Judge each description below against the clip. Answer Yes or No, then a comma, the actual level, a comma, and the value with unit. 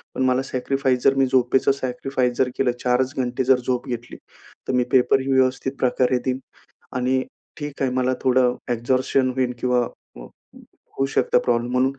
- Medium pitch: No, low, 130 Hz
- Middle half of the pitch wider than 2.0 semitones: No, narrow, 1.1 semitones